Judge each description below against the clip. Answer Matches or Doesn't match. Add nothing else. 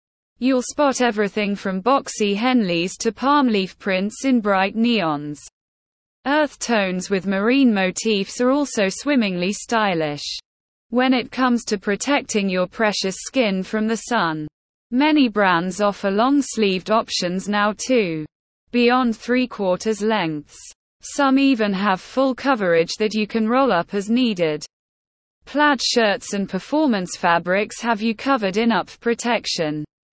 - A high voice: Matches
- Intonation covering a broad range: Doesn't match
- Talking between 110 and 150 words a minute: Matches